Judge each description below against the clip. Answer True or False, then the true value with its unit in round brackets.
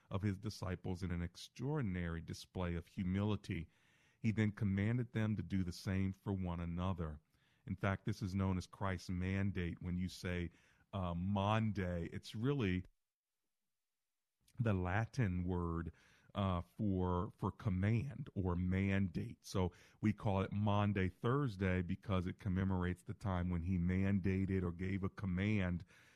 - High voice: False (95 Hz)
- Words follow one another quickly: False (140 wpm)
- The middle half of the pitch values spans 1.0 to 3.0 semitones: True (2.6 semitones)